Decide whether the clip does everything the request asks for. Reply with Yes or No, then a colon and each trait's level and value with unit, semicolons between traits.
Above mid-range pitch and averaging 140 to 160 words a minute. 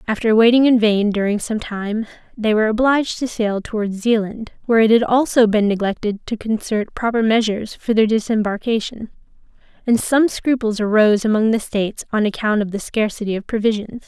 No: high, 220 Hz; average, 175 wpm